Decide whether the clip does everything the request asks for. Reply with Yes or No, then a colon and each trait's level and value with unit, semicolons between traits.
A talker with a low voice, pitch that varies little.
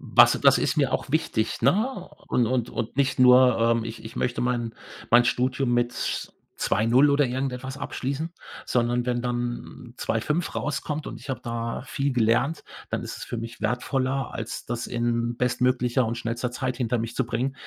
Yes: low, 125 Hz; narrow, 2.1 semitones